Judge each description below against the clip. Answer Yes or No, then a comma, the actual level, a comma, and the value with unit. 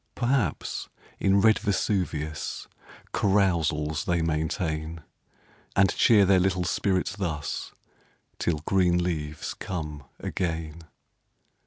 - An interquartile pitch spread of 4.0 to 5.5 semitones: No, average, 3.6 semitones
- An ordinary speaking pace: No, slow, 95 wpm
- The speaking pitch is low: Yes, very low, 85 Hz